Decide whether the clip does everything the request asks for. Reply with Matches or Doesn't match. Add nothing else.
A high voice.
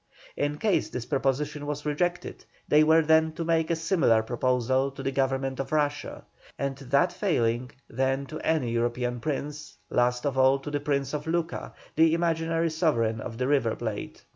Doesn't match